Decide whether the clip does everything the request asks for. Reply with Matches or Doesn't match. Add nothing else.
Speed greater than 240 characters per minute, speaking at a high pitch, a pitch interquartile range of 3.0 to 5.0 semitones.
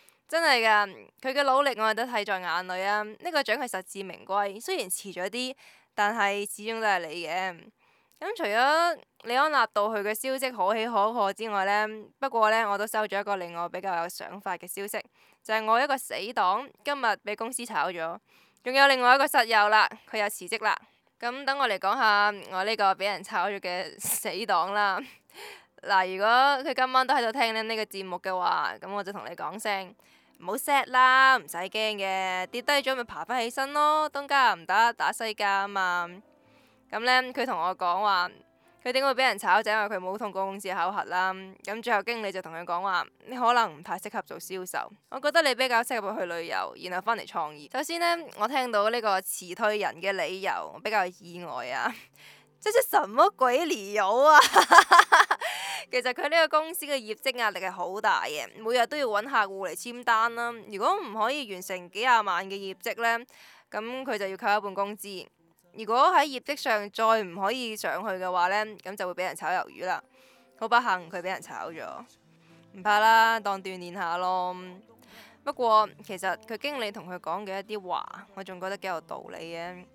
Matches